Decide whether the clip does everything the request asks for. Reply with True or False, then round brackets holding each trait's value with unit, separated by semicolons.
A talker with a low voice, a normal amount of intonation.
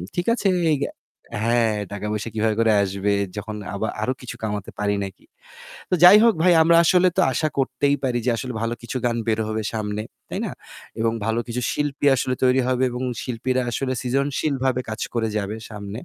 True (120 Hz; 3.5 semitones)